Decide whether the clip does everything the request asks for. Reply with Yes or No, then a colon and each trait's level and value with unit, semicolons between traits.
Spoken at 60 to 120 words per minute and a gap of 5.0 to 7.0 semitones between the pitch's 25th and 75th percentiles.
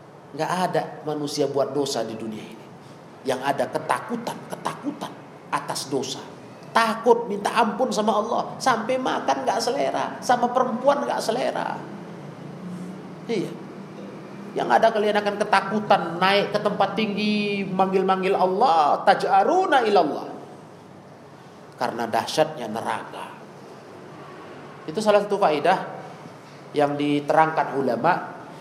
Yes: average, 105 wpm; wide, 5.4 semitones